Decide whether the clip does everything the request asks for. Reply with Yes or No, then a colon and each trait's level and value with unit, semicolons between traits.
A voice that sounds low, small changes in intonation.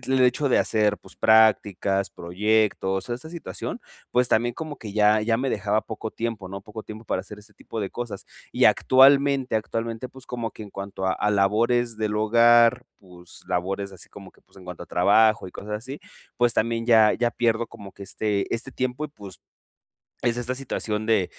No: low, 110 Hz; average, 3.0 semitones